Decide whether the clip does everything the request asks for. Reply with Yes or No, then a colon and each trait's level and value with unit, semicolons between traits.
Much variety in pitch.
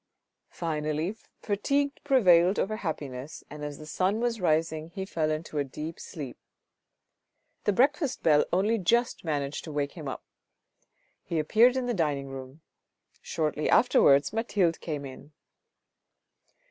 Yes: wide, 5.7 semitones